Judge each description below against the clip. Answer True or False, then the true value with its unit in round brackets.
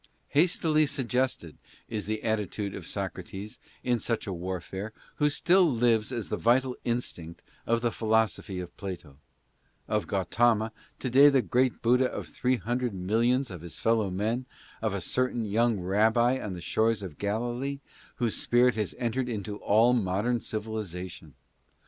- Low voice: True (110 Hz)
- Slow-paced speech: False (155 wpm)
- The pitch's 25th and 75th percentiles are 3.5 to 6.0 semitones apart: True (3.8 semitones)